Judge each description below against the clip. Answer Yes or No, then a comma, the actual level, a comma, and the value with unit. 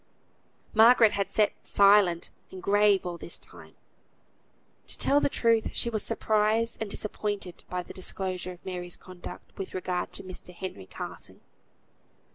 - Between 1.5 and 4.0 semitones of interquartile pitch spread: Yes, average, 2.9 semitones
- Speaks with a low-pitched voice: No, high, 195 Hz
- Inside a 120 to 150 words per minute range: Yes, average, 145 wpm